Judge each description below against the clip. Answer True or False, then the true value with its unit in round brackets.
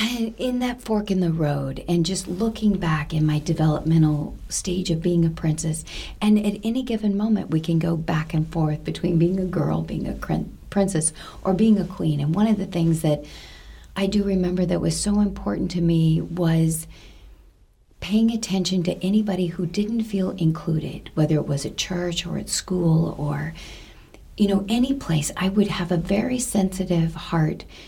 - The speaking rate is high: False (180 wpm)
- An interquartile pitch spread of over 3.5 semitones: True (3.9 semitones)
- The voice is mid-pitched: True (175 Hz)